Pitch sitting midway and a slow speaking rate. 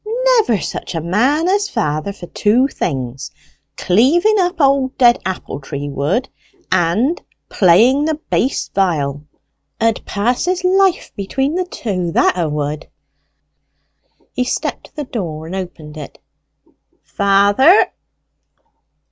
No: high, 215 Hz; slow, 125 wpm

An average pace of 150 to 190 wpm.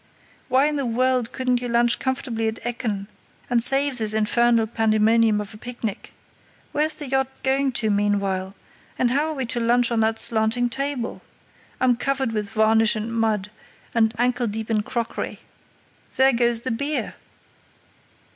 Yes: average, 160 wpm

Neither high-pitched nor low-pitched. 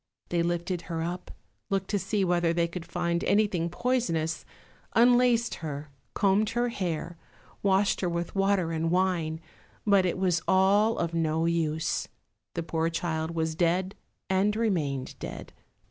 Yes: medium, 175 Hz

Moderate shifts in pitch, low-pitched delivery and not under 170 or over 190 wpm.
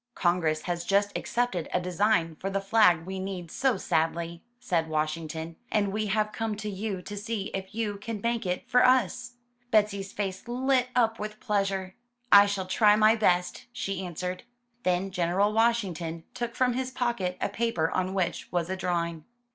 No: average, 3.7 semitones; high, 195 Hz; average, 175 wpm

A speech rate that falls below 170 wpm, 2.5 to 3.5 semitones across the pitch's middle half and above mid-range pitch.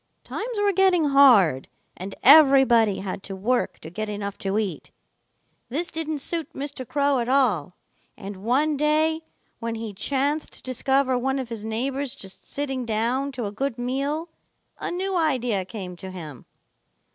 No: average, 160 wpm; wide, 5.5 semitones; very high, 255 Hz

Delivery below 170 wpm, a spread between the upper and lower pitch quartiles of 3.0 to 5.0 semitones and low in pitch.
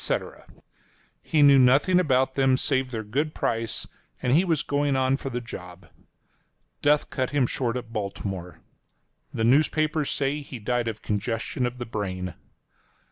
Yes: average, 150 wpm; average, 4.1 semitones; low, 125 Hz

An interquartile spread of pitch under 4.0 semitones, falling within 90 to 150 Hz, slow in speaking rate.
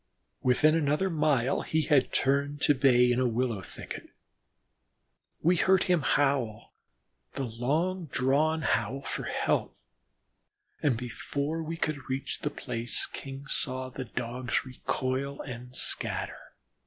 Yes: average, 3.3 semitones; low, 135 Hz; slow, 130 wpm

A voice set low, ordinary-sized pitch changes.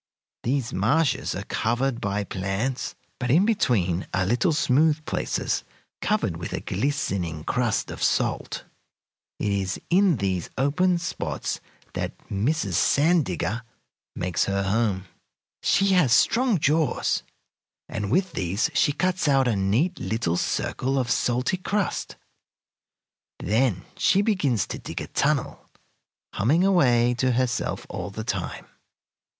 No: low, 125 Hz; wide, 8.1 semitones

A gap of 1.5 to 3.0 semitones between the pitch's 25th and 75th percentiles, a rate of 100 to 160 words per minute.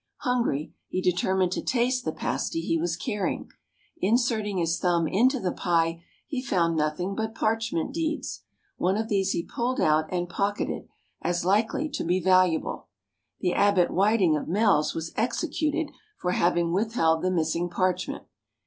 No: average, 4.8 semitones; average, 155 wpm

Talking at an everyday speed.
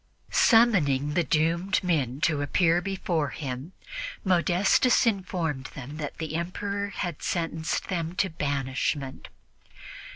No: slow, 110 wpm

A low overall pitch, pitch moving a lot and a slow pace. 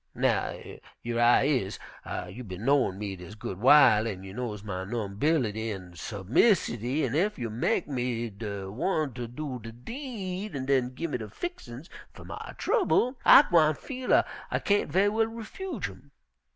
No: low, 125 Hz; wide, 7.9 semitones; average, 175 wpm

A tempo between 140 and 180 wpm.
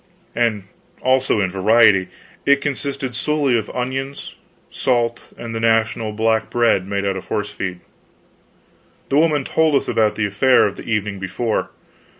Yes: average, 155 wpm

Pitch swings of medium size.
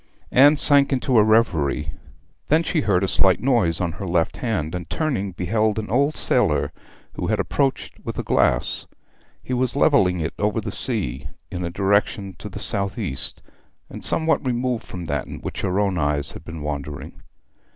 No: wide, 6.6 semitones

